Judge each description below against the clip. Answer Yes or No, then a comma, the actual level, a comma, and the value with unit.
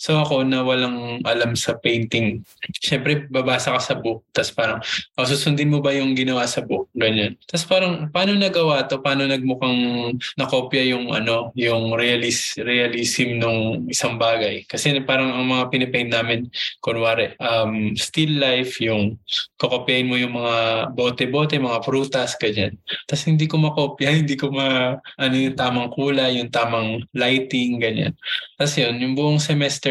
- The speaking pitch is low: Yes, low, 125 Hz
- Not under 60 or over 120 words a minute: No, fast, 155 wpm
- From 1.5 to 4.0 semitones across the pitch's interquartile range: Yes, average, 2.9 semitones